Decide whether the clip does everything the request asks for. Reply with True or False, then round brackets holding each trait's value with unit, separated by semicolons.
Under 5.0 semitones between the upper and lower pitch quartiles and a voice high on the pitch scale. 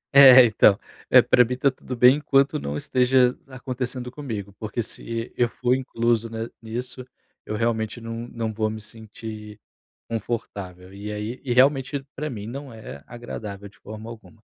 False (2.8 semitones; 115 Hz)